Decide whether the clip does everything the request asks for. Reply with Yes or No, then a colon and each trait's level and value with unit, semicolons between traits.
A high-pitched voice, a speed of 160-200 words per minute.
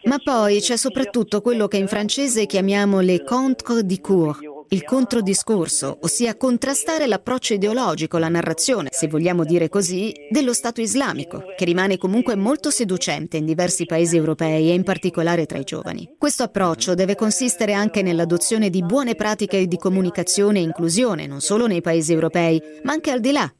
Yes: high, 200 Hz; average, 165 wpm